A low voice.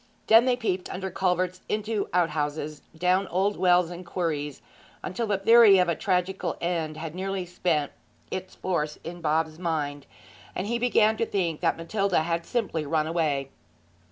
No: medium, 180 Hz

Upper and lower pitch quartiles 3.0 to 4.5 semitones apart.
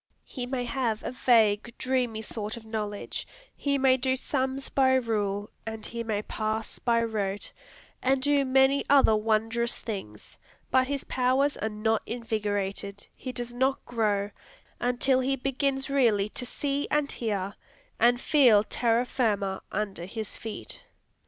Yes: average, 3.6 semitones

